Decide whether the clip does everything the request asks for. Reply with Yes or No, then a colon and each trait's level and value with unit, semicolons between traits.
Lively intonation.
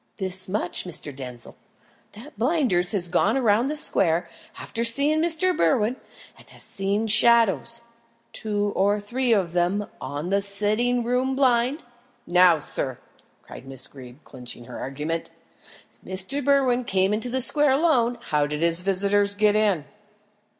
Yes: wide, 5.8 semitones